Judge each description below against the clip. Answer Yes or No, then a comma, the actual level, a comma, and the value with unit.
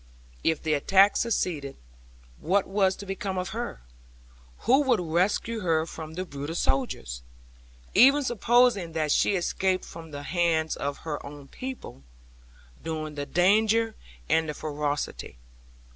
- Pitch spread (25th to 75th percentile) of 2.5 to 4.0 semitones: No, average, 5.0 semitones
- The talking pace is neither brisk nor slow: No, slow, 130 wpm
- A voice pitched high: No, medium, 175 Hz